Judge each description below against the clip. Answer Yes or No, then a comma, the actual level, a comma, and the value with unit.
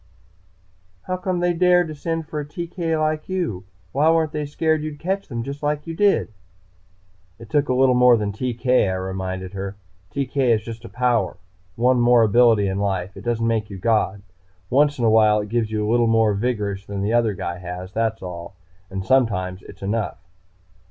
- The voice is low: Yes, low, 115 Hz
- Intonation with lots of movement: Yes, wide, 6.4 semitones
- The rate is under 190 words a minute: No, average, 200 wpm